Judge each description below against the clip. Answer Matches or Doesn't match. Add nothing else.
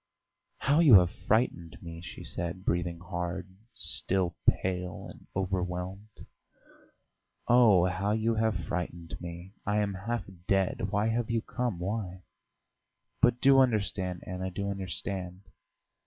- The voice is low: Matches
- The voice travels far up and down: Doesn't match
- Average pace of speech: Doesn't match